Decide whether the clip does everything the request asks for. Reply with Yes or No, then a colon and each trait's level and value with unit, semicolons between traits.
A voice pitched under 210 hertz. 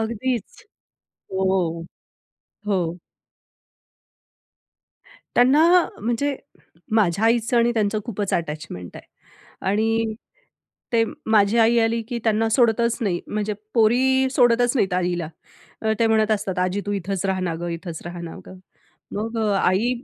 No: high, 220 Hz